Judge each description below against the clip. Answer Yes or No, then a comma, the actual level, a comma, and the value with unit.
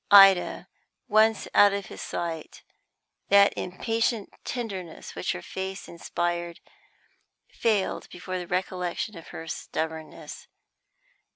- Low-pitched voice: No, medium, 185 Hz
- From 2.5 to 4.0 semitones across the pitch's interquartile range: Yes, average, 2.9 semitones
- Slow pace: Yes, slow, 105 wpm